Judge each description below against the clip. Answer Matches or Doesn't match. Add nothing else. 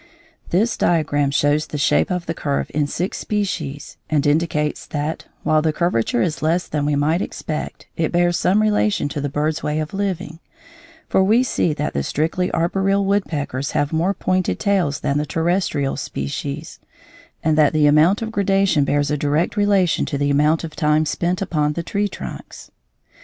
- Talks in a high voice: Doesn't match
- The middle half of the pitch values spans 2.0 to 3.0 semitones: Doesn't match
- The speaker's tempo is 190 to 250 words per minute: Doesn't match